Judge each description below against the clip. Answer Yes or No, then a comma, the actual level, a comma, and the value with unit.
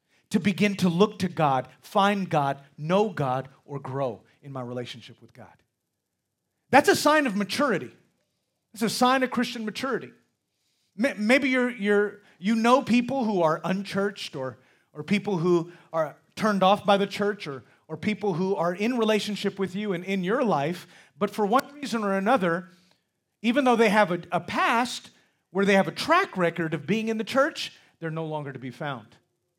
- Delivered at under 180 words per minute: No, average, 185 wpm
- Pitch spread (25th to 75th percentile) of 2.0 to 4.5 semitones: No, wide, 5.5 semitones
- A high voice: Yes, high, 195 Hz